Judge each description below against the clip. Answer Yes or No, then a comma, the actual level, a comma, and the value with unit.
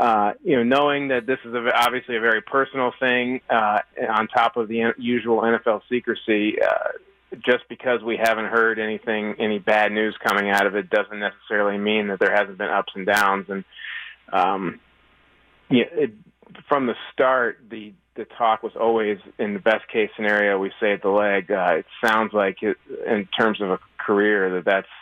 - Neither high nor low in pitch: No, low, 115 Hz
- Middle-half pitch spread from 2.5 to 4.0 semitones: Yes, average, 3.1 semitones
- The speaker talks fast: No, average, 190 wpm